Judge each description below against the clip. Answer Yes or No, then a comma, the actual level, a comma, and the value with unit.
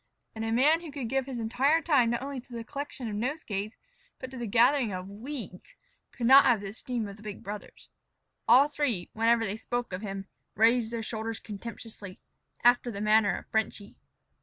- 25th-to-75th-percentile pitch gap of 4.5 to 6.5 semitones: No, average, 3.5 semitones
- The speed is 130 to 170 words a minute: No, average, 195 wpm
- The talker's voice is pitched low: No, high, 230 Hz